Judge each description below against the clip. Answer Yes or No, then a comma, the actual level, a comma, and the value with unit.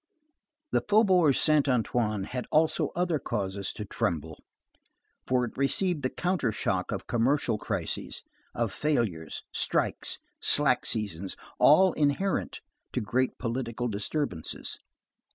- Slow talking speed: Yes, slow, 115 wpm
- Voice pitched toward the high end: No, low, 125 Hz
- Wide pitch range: Yes, wide, 6.2 semitones